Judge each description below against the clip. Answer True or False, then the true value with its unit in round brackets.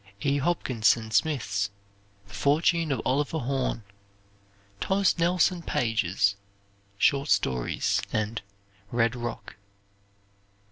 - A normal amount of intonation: False (6.1 semitones)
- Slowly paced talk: True (90 wpm)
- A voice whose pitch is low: True (125 Hz)